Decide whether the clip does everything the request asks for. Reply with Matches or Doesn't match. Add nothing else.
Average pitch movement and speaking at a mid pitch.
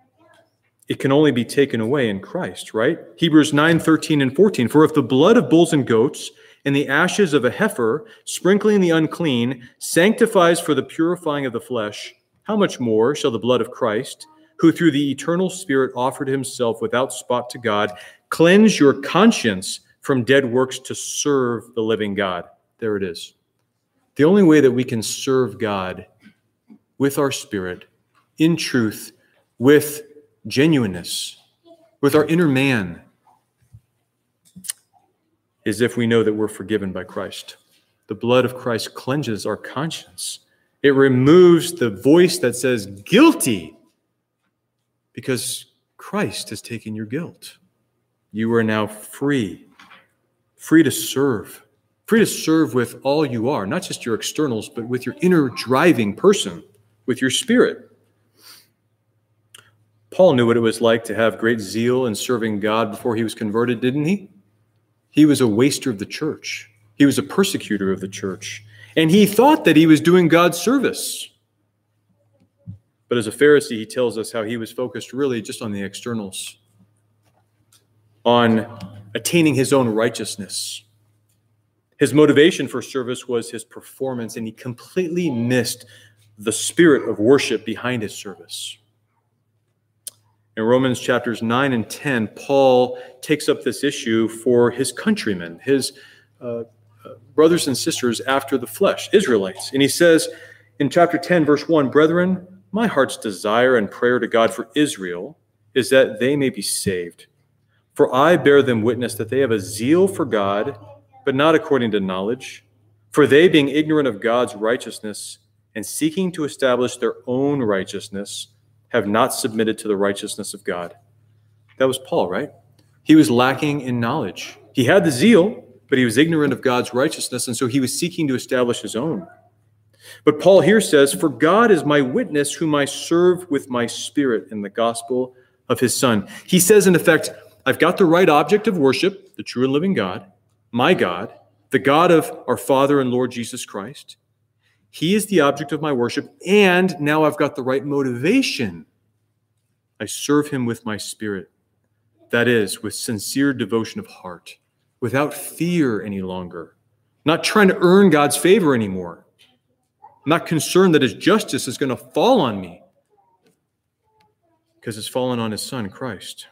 Doesn't match